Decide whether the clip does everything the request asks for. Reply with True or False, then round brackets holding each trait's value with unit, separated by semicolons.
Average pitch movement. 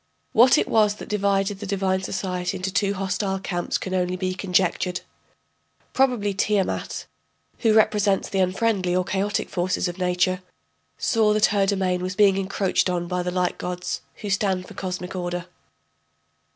False (1.9 semitones)